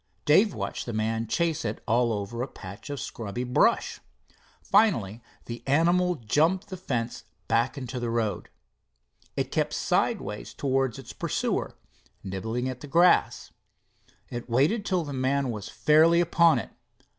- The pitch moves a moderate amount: No, wide, 6.1 semitones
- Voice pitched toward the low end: Yes, low, 130 Hz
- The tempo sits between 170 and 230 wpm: No, average, 145 wpm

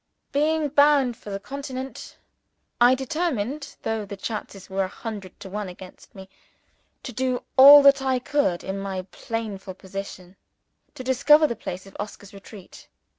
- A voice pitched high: Yes, high, 225 Hz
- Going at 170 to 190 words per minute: No, average, 155 wpm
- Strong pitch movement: Yes, wide, 5.8 semitones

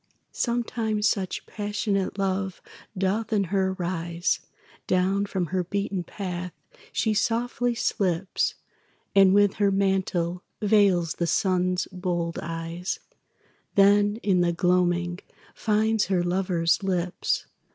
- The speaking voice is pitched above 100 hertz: Yes, high, 190 Hz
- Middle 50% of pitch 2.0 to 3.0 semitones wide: Yes, narrow, 2.5 semitones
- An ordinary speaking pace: No, slow, 110 wpm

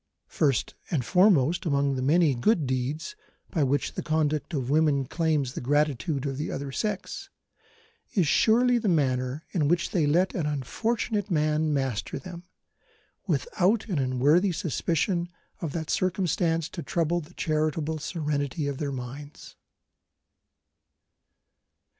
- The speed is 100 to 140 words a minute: Yes, slow, 135 wpm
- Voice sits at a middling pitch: Yes, medium, 155 Hz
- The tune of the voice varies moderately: Yes, average, 3.8 semitones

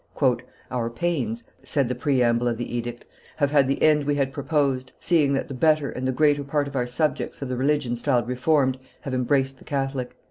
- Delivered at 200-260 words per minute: Yes, fast, 205 wpm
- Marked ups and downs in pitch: No, average, 2.7 semitones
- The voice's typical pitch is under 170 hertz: Yes, low, 135 Hz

